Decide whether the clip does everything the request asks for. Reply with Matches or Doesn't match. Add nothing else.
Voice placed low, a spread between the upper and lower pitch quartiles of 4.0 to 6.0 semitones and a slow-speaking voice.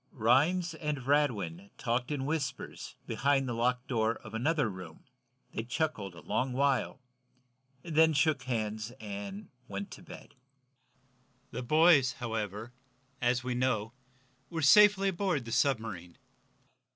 Matches